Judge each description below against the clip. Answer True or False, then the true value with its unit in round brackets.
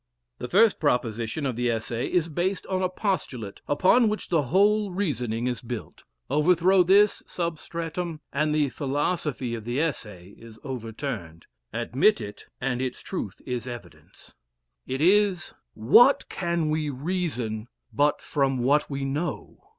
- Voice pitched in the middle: True (145 Hz)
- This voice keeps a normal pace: True (145 wpm)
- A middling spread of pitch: False (6.6 semitones)